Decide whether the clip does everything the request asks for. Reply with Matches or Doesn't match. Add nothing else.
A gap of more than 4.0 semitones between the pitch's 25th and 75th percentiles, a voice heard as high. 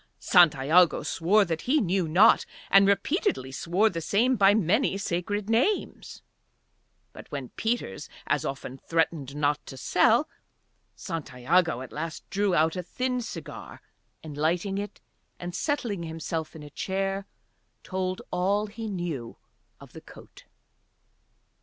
Doesn't match